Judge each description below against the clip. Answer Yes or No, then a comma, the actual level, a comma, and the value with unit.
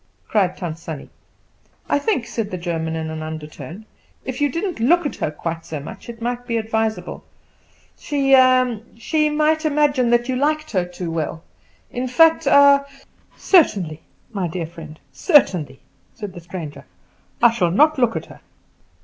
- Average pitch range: No, wide, 9.0 semitones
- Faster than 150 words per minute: Yes, average, 165 wpm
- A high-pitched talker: Yes, high, 225 Hz